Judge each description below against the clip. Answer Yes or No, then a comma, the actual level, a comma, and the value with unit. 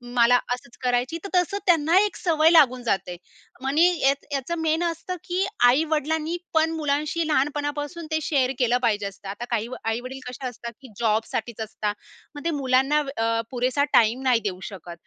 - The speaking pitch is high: Yes, very high, 265 Hz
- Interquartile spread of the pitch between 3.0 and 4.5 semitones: No, average, 5.0 semitones